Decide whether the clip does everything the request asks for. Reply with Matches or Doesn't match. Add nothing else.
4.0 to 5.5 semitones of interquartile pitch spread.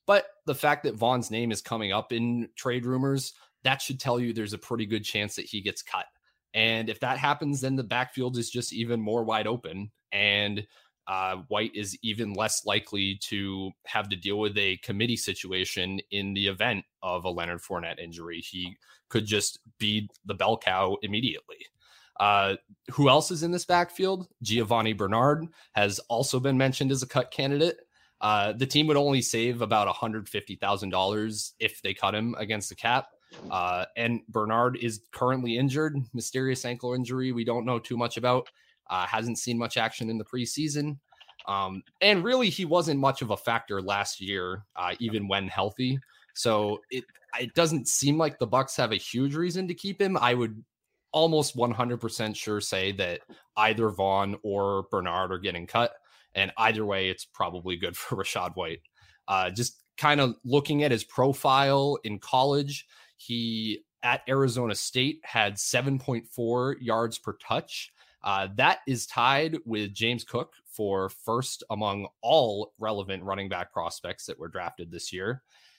Matches